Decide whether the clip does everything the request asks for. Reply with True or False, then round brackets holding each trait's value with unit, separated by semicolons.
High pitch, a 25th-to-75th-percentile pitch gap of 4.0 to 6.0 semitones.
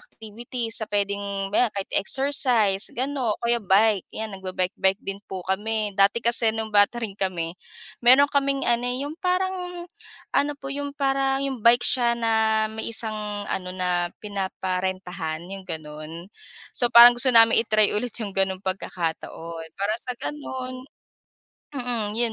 True (220 Hz; 4.5 semitones)